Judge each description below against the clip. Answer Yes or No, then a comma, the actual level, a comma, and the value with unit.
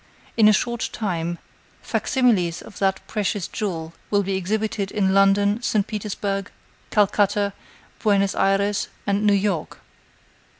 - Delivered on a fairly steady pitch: Yes, narrow, 1.6 semitones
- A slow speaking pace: Yes, slow, 130 wpm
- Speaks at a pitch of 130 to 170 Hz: No, high, 200 Hz